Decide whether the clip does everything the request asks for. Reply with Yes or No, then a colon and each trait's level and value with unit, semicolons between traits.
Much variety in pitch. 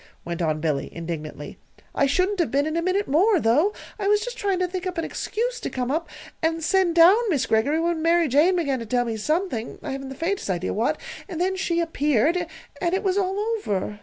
Yes: wide, 7.1 semitones